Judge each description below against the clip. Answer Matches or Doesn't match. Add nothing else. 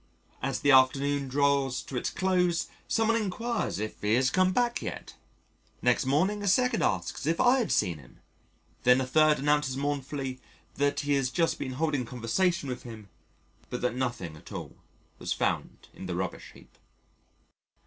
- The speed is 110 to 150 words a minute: Doesn't match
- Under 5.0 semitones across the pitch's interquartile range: Doesn't match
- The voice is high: Doesn't match